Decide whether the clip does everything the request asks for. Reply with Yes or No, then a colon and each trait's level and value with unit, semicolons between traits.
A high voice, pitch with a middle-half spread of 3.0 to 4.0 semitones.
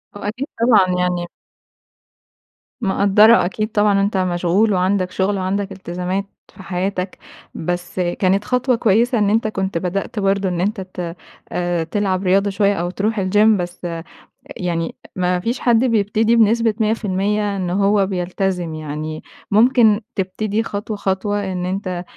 No: high, 195 Hz; narrow, 2.6 semitones